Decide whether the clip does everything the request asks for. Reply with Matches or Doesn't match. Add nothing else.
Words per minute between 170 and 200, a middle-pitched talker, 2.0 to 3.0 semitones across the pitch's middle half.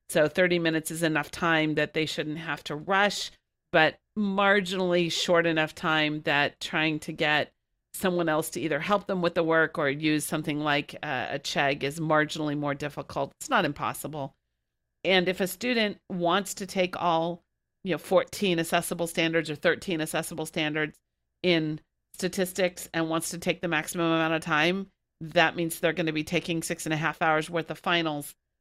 Matches